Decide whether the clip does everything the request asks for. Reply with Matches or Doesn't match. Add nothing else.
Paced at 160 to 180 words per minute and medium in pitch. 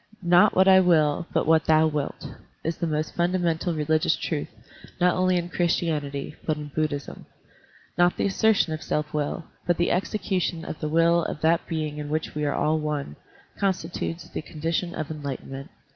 Matches